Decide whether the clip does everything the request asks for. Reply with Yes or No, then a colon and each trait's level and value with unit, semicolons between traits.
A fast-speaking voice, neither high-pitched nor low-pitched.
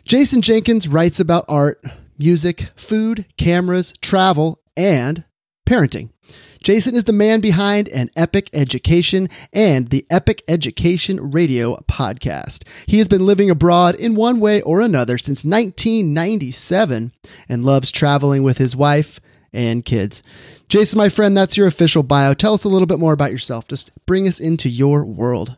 No: average, 155 wpm; medium, 170 Hz